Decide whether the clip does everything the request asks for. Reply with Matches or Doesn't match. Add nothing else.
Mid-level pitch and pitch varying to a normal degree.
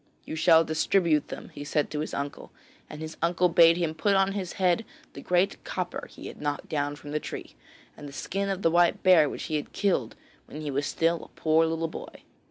Matches